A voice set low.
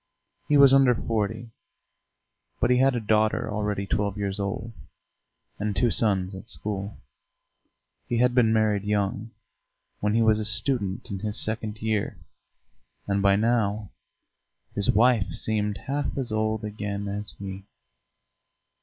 Yes: low, 105 Hz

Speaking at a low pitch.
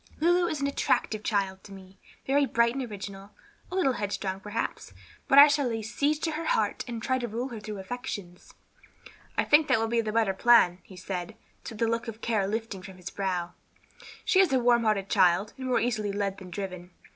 No: high, 220 Hz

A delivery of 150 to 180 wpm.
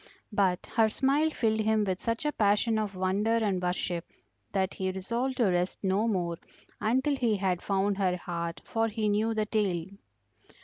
Yes: average, 175 wpm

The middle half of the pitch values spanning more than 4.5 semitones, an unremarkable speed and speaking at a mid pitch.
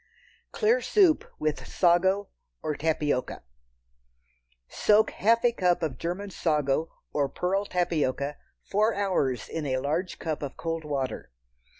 No: average, 5.3 semitones; slow, 125 wpm; medium, 165 Hz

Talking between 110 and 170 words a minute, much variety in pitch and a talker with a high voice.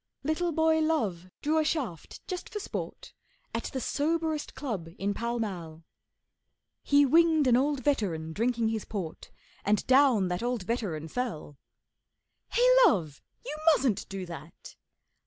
Yes: average, 140 wpm; wide, 8.3 semitones; high, 240 Hz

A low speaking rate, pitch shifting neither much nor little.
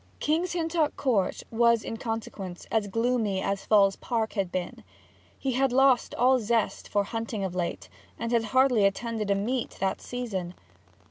No: average, 160 wpm; average, 3.9 semitones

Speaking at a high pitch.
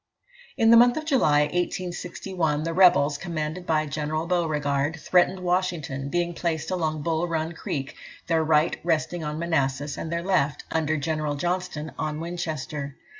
No: medium, 160 Hz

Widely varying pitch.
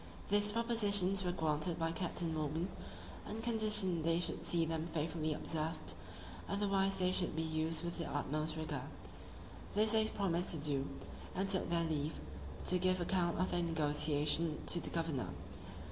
No: average, 3.3 semitones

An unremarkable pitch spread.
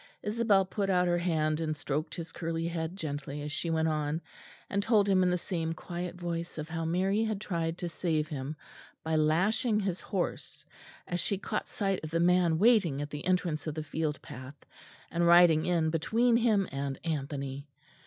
Yes: average, 3.2 semitones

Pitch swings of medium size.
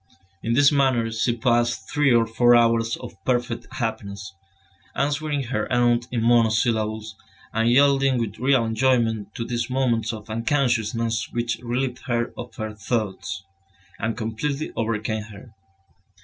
No: narrow, 2.1 semitones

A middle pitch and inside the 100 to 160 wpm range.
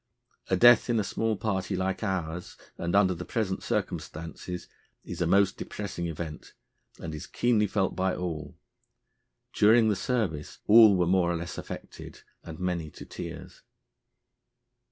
No: very low, 95 Hz; average, 150 wpm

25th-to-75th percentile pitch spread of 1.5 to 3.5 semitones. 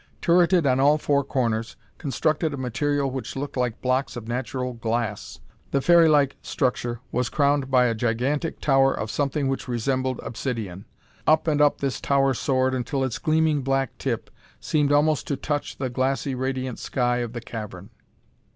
Yes: average, 2.8 semitones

